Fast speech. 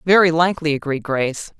No: average, 150 wpm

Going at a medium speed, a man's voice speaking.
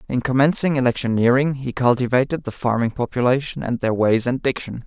Yes: average, 160 wpm; male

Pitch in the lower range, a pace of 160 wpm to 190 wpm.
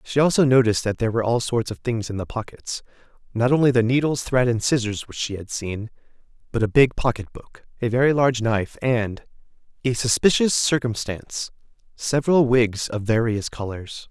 Yes: low, 120 Hz; average, 170 wpm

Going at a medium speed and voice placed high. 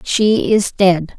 Yes: average, 150 wpm; high, 195 Hz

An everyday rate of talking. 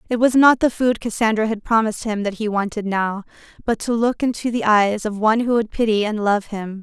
No: fast, 235 wpm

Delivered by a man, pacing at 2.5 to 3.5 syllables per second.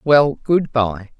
No: female; 2.9 syllables/s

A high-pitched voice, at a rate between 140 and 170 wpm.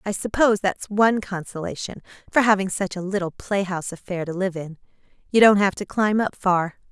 No: high, 195 Hz; average, 190 wpm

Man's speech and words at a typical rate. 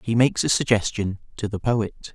Yes: male; average, 195 wpm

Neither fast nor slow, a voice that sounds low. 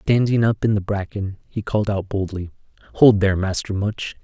Yes: average, 185 wpm; low, 100 Hz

